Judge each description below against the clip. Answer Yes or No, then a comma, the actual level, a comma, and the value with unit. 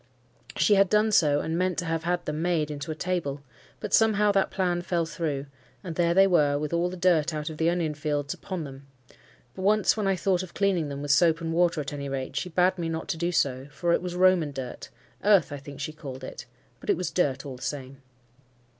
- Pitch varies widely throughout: No, average, 3.8 semitones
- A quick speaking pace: Yes, fast, 235 wpm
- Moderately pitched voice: Yes, medium, 165 Hz